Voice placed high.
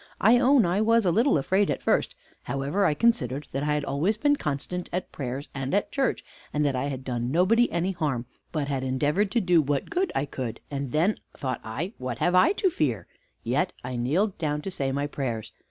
No: medium, 150 Hz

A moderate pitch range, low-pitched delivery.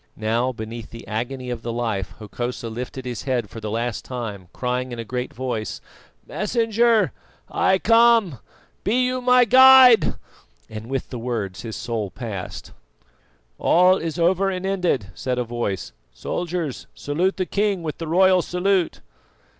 No: wide, 8.6 semitones; low, 130 Hz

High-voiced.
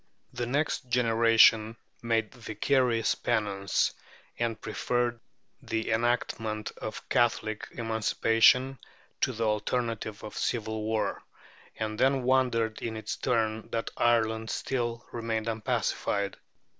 No: low, 115 Hz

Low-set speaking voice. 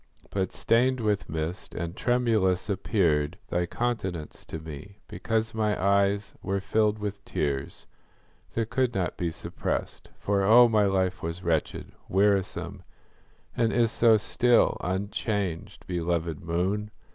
Yes: low, 100 Hz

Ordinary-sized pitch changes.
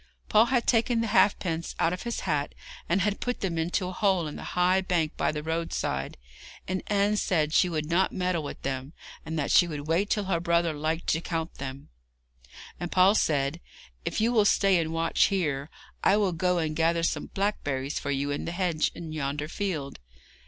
Yes: average, 3.8 semitones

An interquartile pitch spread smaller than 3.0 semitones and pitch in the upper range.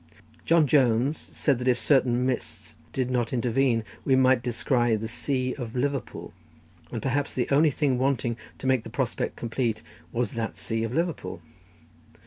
No: narrow, 2.5 semitones; low, 125 Hz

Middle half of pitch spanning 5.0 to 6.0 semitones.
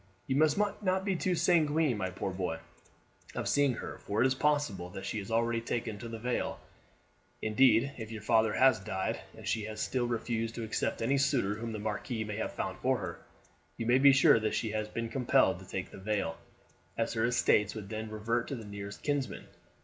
No: average, 3.7 semitones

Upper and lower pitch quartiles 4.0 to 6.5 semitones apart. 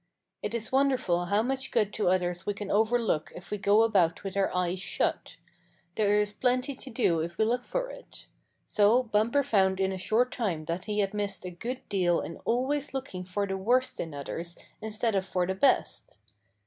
Yes: average, 4.7 semitones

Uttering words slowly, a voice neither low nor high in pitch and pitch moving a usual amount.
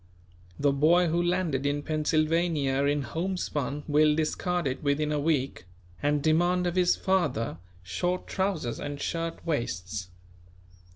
Yes: slow, 130 wpm; medium, 155 Hz; average, 3.6 semitones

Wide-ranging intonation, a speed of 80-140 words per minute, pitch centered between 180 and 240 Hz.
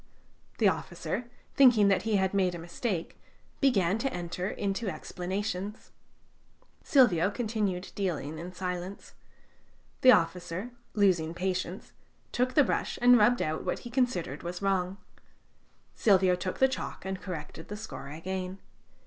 No: average, 3.5 semitones; slow, 135 wpm; high, 190 Hz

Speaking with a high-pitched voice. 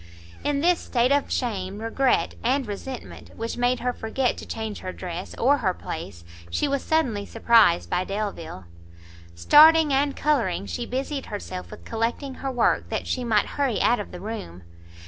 Yes: high, 230 Hz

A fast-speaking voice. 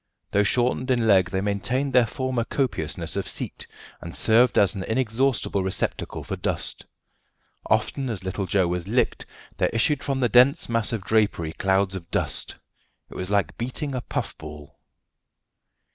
No: average, 160 wpm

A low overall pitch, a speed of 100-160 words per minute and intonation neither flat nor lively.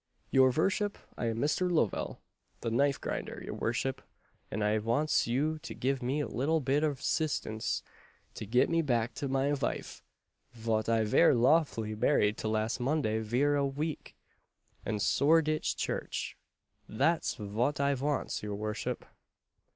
Yes: low, 130 Hz; average, 150 wpm; average, 4.8 semitones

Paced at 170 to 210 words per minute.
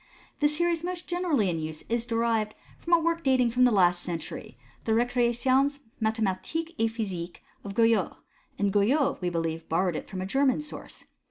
Yes: average, 180 wpm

